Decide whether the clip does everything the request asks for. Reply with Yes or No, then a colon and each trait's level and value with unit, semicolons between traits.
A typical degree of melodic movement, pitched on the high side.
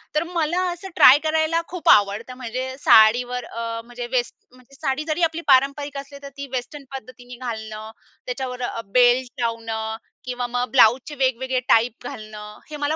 Yes: average, 3.4 semitones; very high, 250 Hz